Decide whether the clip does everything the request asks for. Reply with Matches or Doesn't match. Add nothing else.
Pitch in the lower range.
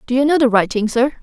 Doesn't match